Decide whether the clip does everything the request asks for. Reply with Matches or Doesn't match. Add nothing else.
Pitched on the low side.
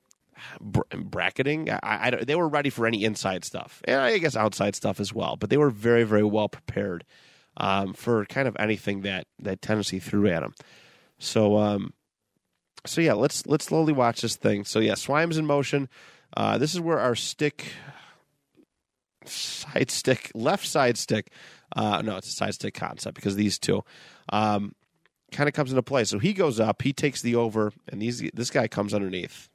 Matches